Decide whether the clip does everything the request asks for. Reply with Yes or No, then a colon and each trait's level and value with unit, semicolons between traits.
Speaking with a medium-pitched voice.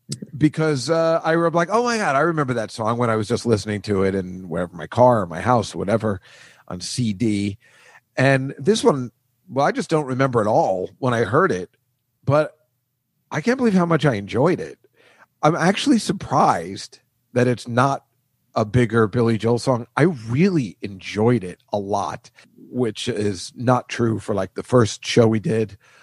No: low, 125 Hz